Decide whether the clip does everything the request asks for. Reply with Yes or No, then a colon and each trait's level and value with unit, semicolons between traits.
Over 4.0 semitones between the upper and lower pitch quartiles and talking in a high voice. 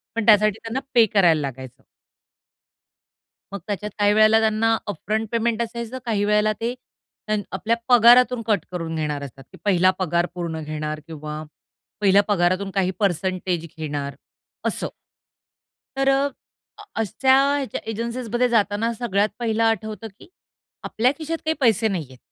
Yes: average, 4.7 semitones; high, 210 Hz